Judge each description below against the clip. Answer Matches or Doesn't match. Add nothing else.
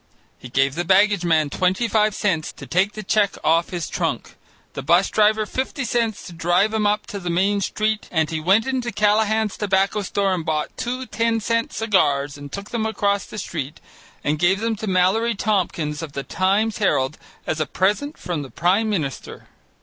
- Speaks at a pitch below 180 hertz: Doesn't match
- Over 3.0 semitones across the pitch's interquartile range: Matches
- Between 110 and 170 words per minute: Doesn't match